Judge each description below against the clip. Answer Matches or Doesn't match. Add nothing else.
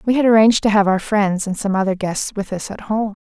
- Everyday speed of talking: Doesn't match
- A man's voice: Doesn't match